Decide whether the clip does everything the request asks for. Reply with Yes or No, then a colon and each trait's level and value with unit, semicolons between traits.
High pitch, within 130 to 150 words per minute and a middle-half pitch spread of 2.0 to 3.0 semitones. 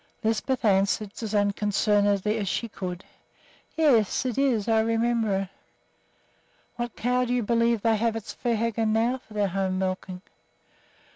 Yes: high, 220 Hz; average, 145 wpm; average, 2.7 semitones